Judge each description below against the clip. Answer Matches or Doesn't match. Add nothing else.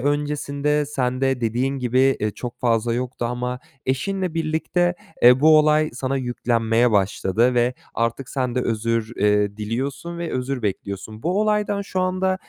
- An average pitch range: Matches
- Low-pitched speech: Matches